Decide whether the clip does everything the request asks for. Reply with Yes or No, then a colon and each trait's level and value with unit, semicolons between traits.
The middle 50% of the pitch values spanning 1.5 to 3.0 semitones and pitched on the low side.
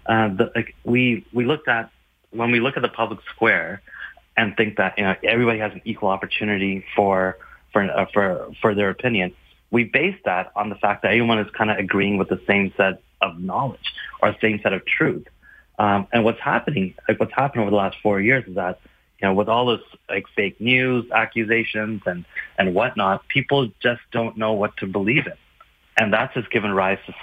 Yes: average, 2.7 semitones; low, 110 Hz